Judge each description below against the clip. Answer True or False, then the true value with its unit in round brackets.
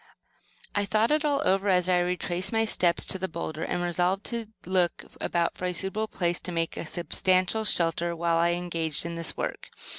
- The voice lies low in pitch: False (180 Hz)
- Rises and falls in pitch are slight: True (2.3 semitones)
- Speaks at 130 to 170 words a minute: False (190 wpm)